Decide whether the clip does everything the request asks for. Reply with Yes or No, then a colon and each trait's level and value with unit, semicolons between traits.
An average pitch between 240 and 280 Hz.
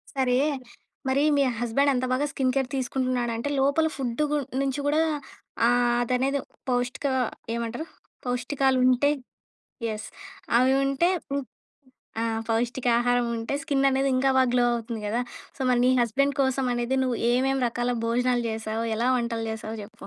Yes: very high, 250 Hz